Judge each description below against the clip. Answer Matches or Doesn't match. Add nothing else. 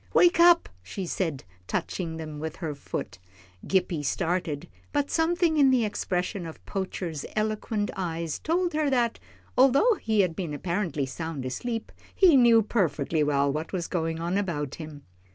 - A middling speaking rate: Matches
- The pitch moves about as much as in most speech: Doesn't match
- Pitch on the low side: Doesn't match